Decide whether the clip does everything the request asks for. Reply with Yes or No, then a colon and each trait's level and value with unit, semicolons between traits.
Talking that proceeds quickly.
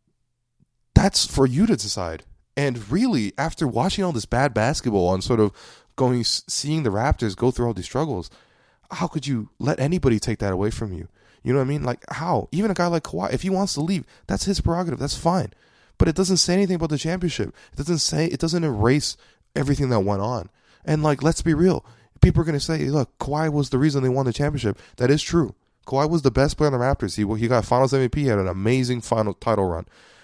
Yes: fast, 230 wpm